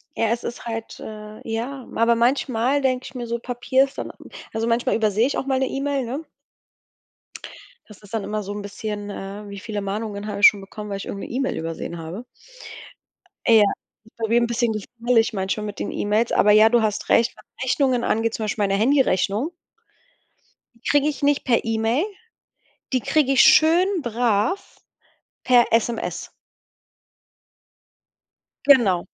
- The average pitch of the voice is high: Yes, high, 230 Hz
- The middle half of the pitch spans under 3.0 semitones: No, average, 3.3 semitones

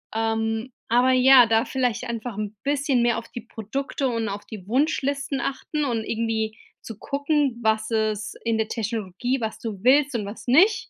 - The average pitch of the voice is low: No, high, 235 Hz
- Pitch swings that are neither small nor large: Yes, average, 3.3 semitones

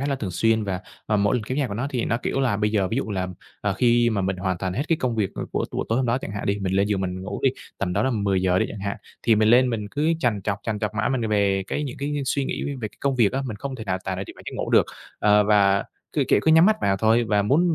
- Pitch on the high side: No, low, 105 Hz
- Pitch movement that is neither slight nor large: Yes, average, 4.4 semitones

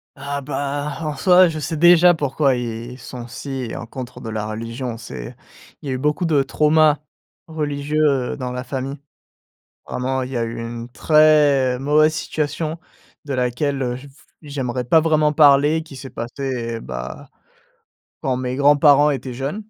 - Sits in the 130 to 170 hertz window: Yes, medium, 140 Hz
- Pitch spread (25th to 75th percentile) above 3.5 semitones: No, average, 3.2 semitones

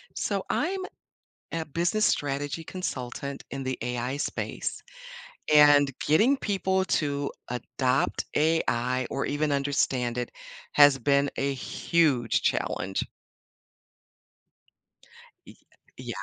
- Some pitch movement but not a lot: Yes, average, 3.6 semitones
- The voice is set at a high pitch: No, medium, 140 Hz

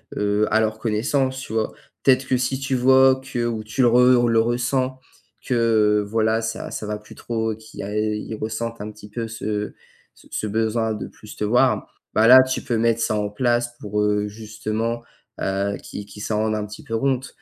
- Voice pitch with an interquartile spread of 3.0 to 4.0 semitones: No, narrow, 2.4 semitones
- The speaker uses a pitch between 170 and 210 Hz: No, low, 110 Hz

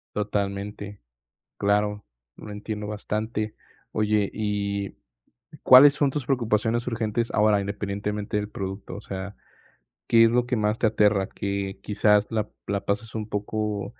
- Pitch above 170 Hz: No, low, 105 Hz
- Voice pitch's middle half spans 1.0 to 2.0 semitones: Yes, narrow, 1.3 semitones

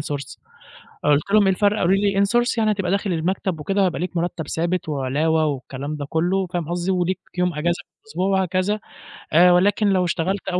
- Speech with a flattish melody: No, average, 3.3 semitones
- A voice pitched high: No, medium, 180 Hz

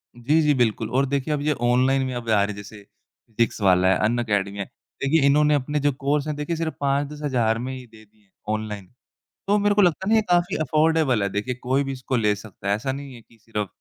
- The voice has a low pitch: Yes, low, 130 Hz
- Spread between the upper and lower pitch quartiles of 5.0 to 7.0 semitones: Yes, wide, 5.4 semitones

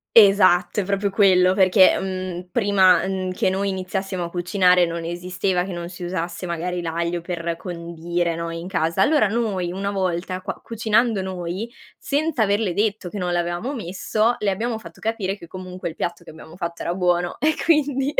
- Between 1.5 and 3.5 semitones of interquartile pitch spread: Yes, narrow, 2.6 semitones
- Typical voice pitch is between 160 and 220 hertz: Yes, medium, 185 Hz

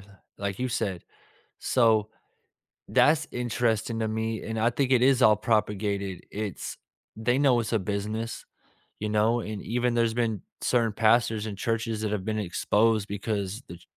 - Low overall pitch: Yes, low, 110 Hz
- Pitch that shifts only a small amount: Yes, narrow, 2.1 semitones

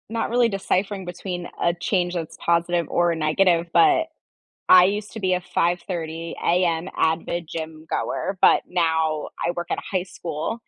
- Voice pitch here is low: No, medium, 175 Hz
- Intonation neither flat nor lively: No, narrow, 2.3 semitones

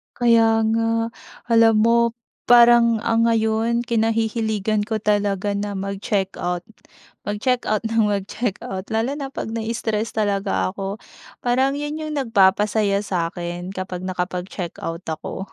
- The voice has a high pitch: Yes, high, 215 Hz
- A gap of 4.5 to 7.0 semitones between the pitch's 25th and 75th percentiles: No, average, 2.9 semitones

